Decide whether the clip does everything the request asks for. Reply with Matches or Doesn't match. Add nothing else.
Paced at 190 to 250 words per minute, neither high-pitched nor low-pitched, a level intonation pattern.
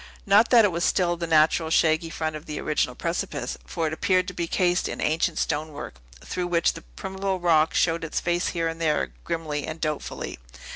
Matches